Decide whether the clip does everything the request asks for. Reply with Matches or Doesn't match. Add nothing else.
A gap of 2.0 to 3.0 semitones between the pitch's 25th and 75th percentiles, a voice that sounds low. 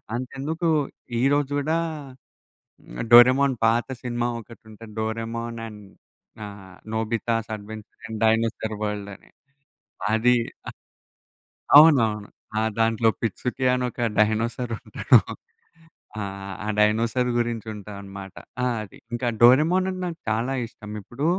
Matches